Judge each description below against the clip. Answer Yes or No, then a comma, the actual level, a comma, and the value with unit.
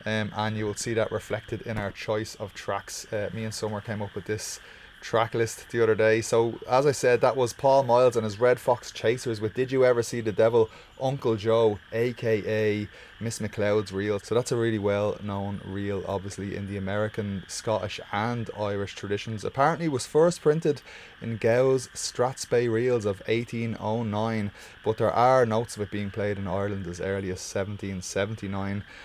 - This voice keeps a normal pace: Yes, average, 190 wpm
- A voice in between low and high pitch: No, low, 110 Hz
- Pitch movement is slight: Yes, narrow, 2.3 semitones